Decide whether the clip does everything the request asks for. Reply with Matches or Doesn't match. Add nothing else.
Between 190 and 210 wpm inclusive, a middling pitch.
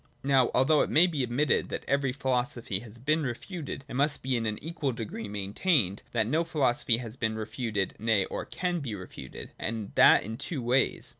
Doesn't match